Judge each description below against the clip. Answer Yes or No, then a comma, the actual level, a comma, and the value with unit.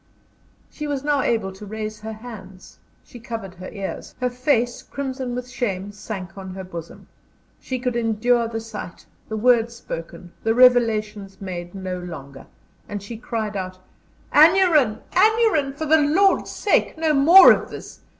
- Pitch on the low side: No, high, 225 Hz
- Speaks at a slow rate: No, average, 160 wpm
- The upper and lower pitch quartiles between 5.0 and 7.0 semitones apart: Yes, average, 5.3 semitones